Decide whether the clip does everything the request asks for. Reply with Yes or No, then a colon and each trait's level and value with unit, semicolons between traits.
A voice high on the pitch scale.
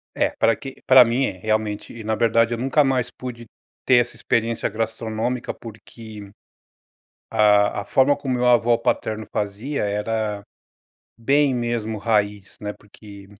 No: low, 115 Hz